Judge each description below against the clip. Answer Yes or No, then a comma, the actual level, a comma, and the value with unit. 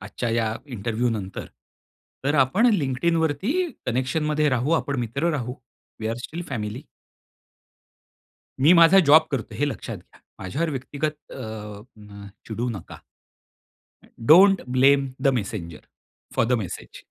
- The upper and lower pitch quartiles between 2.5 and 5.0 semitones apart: No, wide, 5.6 semitones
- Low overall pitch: Yes, low, 130 Hz